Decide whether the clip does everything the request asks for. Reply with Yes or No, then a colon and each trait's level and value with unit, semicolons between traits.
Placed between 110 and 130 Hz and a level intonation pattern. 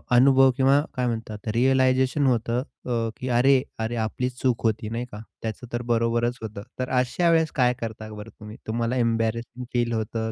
Yes: low, 120 Hz; narrow, 2.2 semitones